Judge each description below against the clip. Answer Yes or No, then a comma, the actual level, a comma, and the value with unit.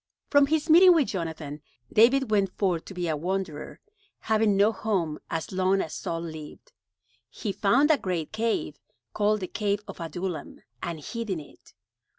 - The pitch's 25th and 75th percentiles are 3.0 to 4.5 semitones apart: No, average, 5.0 semitones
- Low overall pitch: No, high, 195 Hz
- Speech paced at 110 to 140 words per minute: No, average, 165 wpm